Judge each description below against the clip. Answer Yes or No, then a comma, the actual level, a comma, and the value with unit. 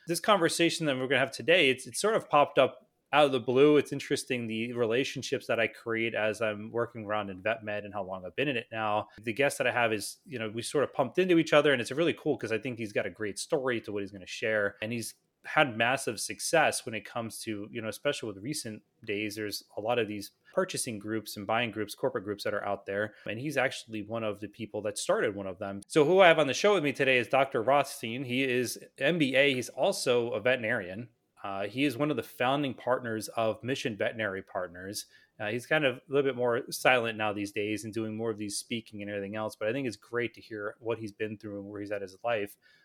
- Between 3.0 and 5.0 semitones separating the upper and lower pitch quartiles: Yes, average, 4.1 semitones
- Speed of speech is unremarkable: No, fast, 260 wpm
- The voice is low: Yes, low, 115 Hz